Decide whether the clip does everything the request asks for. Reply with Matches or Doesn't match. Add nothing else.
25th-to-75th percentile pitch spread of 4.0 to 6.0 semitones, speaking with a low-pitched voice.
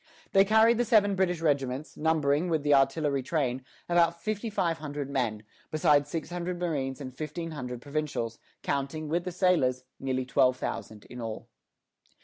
Doesn't match